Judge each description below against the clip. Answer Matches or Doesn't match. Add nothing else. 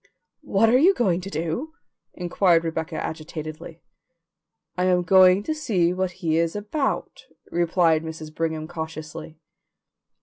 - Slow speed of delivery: Matches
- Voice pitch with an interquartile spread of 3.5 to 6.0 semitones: Doesn't match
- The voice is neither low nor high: Matches